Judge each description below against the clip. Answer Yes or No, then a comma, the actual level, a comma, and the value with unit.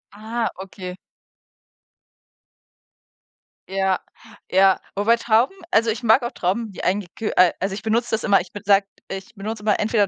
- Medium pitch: No, high, 210 Hz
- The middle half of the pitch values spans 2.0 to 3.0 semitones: Yes, narrow, 2.6 semitones